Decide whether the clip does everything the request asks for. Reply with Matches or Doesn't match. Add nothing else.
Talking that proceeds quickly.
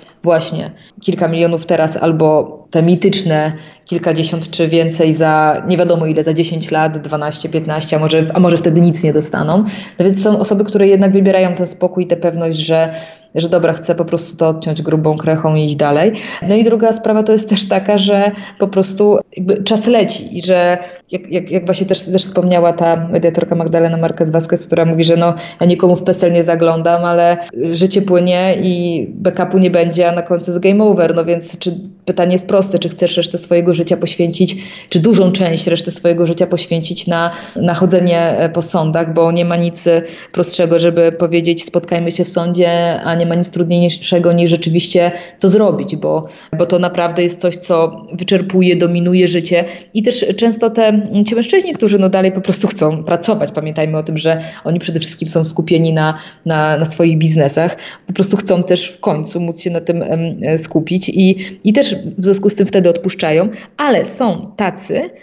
Matches